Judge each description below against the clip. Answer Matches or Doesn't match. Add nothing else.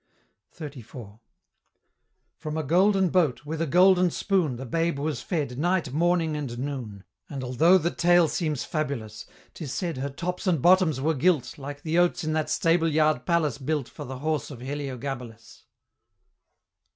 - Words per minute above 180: Doesn't match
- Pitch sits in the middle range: Matches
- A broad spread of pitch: Doesn't match